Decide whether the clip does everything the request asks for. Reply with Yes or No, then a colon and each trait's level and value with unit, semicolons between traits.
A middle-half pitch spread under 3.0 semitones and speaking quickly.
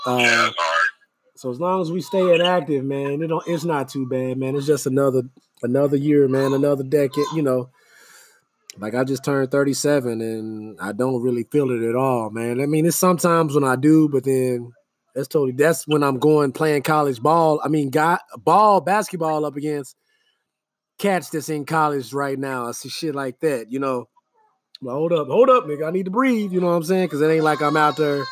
No: average, 3.6 semitones; fast, 215 wpm